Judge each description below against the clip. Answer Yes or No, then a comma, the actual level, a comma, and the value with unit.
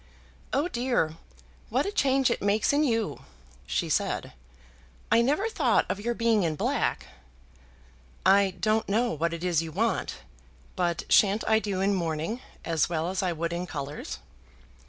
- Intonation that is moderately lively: No, wide, 5.8 semitones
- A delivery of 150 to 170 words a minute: Yes, average, 160 wpm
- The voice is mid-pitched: No, high, 200 Hz